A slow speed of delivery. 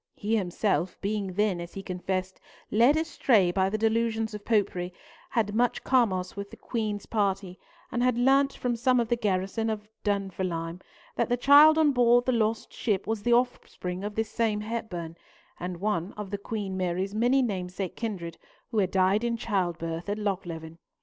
No: average, 175 wpm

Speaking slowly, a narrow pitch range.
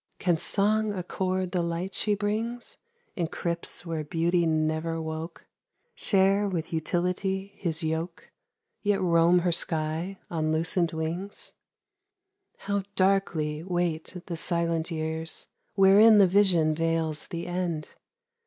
No: slow, 120 wpm; average, 3.0 semitones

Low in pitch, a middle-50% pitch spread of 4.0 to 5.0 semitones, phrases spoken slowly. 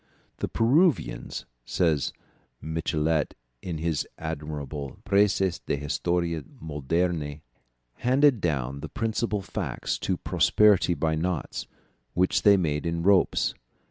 Yes: very low, 85 Hz; average, 4.3 semitones; slow, 105 wpm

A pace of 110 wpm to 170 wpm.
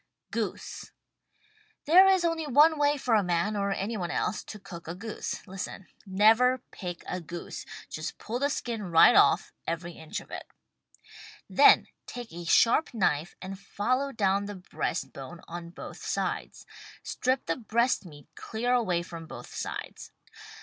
Yes: average, 165 wpm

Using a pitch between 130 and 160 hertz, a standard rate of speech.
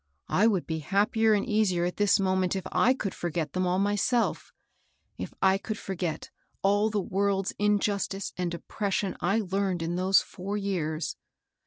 No: high, 195 Hz; average, 170 wpm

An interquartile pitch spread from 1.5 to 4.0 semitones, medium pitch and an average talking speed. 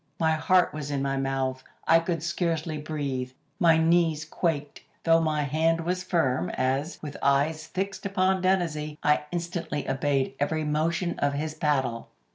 Yes: average, 2.8 semitones; medium, 155 Hz; average, 155 wpm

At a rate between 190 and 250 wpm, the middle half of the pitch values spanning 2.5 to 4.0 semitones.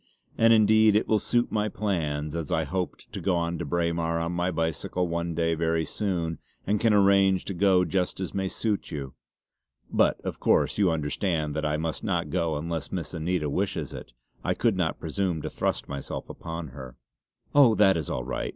Yes: average, 195 wpm; average, 3.4 semitones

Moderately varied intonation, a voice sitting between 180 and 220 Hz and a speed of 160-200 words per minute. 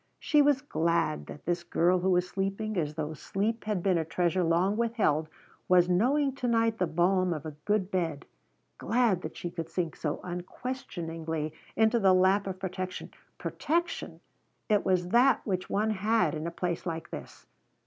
Yes: average, 4.2 semitones; medium, 185 Hz; average, 175 wpm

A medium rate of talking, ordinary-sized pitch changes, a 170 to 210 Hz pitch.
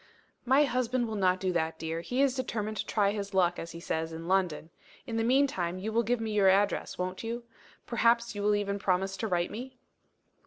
No: fast, 225 wpm; average, 4.4 semitones; high, 205 Hz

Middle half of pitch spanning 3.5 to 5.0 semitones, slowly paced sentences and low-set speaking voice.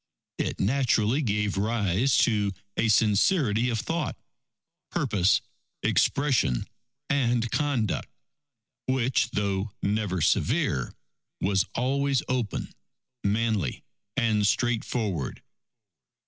Yes: average, 4.0 semitones; slow, 85 wpm; low, 110 Hz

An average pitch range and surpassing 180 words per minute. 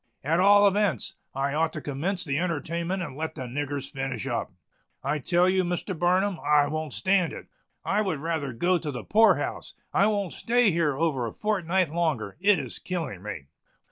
Yes: average, 4.8 semitones; average, 190 wpm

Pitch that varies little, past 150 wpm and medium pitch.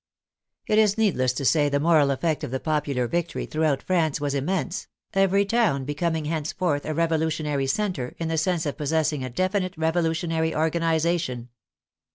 No: average, 3.1 semitones; average, 160 wpm; medium, 160 Hz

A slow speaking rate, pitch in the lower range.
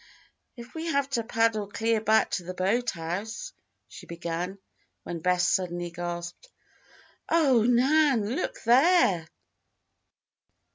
No: slow, 110 wpm; high, 220 Hz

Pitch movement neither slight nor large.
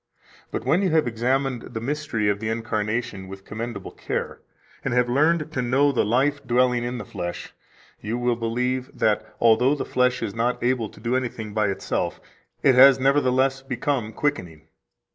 Yes: average, 3.2 semitones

